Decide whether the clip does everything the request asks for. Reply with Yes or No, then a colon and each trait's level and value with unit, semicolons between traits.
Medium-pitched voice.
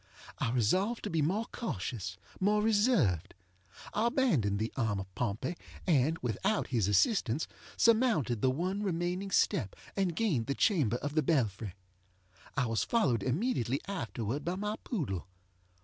Yes: medium, 145 Hz